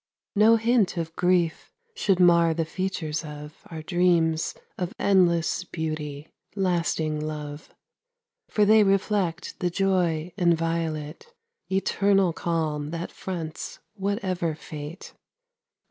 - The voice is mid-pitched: Yes, medium, 170 Hz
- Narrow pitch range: No, average, 3.2 semitones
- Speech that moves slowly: Yes, slow, 105 wpm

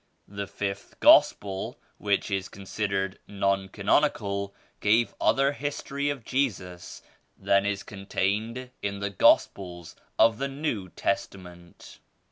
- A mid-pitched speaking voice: No, low, 100 Hz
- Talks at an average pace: No, slow, 115 wpm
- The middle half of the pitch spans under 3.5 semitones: Yes, average, 2.9 semitones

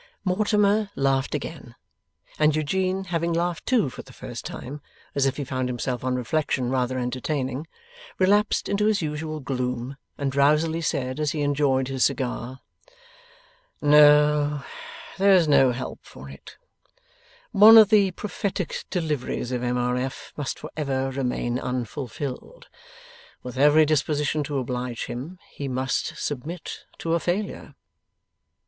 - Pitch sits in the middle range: Yes, medium, 145 Hz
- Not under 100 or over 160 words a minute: Yes, average, 140 wpm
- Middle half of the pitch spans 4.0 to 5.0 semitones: Yes, average, 4.4 semitones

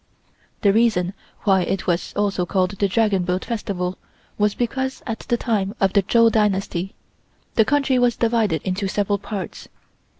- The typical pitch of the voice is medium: No, high, 205 Hz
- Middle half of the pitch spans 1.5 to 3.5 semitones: Yes, average, 3.1 semitones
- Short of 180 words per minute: Yes, average, 160 wpm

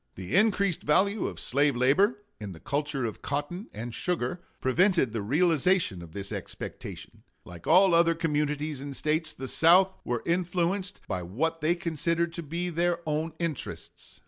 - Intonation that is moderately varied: Yes, average, 4.7 semitones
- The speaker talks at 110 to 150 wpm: No, average, 160 wpm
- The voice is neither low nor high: Yes, medium, 160 Hz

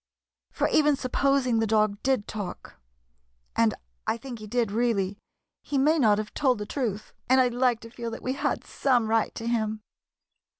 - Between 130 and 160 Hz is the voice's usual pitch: No, high, 230 Hz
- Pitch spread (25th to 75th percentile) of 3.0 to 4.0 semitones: Yes, average, 3.3 semitones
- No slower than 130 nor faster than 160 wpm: No, average, 200 wpm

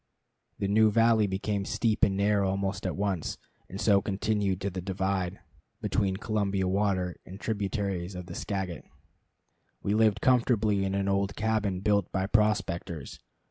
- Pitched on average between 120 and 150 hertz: No, low, 100 Hz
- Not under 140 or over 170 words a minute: Yes, average, 150 wpm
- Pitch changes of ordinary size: No, narrow, 1.8 semitones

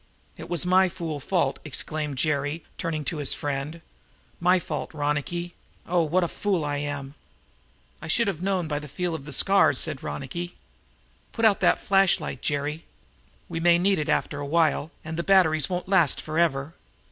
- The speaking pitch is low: No, medium, 160 Hz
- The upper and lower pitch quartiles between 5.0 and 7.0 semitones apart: No, average, 3.3 semitones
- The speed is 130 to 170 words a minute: No, average, 180 wpm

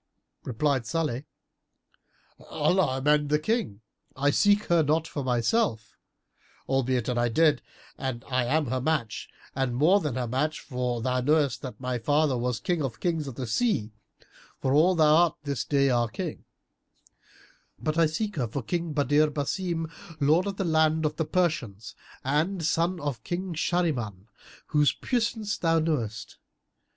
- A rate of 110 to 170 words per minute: Yes, average, 160 wpm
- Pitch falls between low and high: Yes, medium, 150 Hz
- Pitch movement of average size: Yes, average, 4.5 semitones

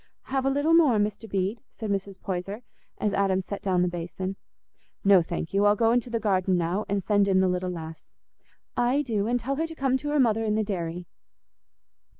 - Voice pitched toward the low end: No, high, 205 Hz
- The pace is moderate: No, fast, 210 wpm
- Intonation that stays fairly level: No, average, 4.3 semitones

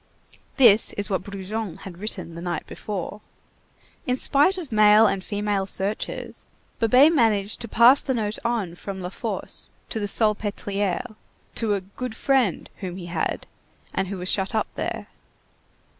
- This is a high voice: Yes, high, 210 Hz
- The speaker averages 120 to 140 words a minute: No, average, 160 wpm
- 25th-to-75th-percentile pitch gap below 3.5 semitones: Yes, average, 3.0 semitones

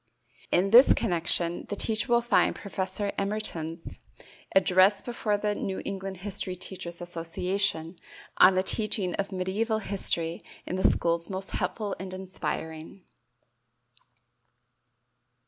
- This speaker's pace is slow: Yes, slow, 115 wpm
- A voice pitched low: No, high, 190 Hz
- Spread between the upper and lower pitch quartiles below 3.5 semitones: Yes, average, 2.7 semitones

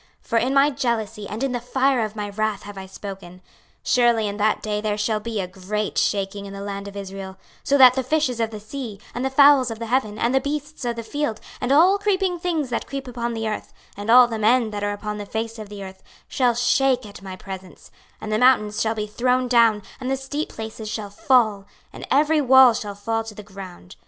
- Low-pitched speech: No, high, 225 Hz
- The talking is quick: Yes, fast, 240 wpm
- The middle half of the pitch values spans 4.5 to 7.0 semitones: No, average, 3.9 semitones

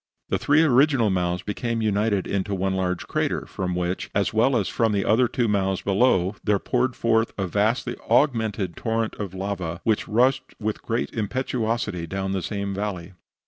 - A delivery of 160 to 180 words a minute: Yes, average, 175 wpm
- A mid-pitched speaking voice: No, low, 105 Hz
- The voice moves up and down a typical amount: Yes, average, 3.4 semitones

